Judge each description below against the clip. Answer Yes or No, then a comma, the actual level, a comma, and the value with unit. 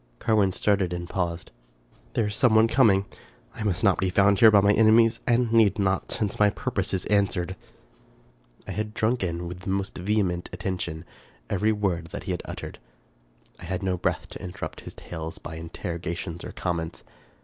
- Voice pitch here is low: Yes, very low, 95 Hz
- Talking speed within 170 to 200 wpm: Yes, average, 185 wpm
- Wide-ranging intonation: No, average, 3.3 semitones